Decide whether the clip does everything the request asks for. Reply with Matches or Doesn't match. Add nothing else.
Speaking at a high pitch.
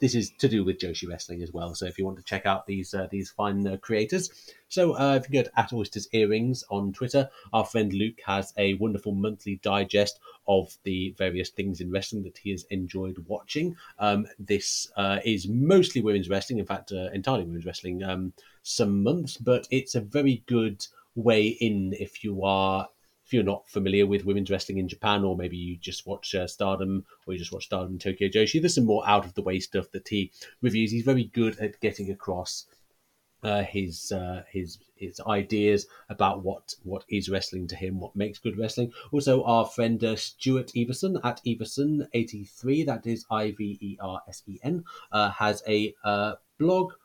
Doesn't match